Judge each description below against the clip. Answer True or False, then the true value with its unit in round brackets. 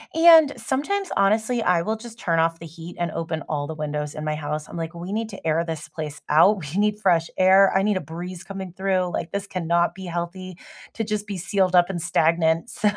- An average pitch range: True (3.6 semitones)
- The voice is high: False (175 Hz)